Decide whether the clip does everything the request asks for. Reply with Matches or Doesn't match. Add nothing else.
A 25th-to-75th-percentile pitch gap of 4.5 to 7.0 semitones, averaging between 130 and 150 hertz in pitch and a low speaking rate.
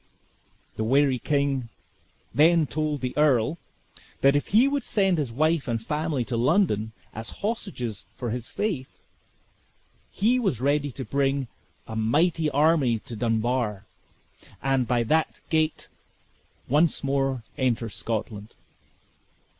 Matches